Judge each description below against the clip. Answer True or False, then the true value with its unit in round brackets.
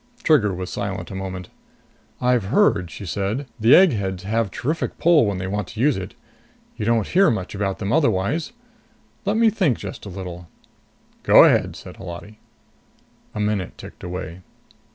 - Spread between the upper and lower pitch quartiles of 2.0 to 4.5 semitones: False (5.0 semitones)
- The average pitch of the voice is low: True (105 Hz)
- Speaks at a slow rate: False (165 wpm)